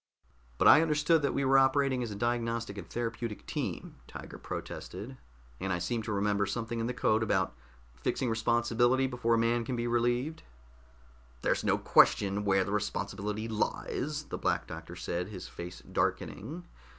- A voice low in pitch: Yes, low, 115 Hz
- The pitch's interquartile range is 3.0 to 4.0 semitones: Yes, average, 3.6 semitones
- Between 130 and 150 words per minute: No, average, 165 wpm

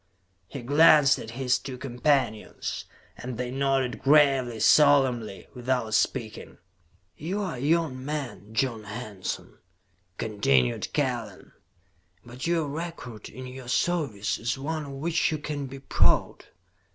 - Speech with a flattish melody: No, average, 3.8 semitones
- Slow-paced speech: Yes, slow, 130 wpm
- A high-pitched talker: No, low, 130 Hz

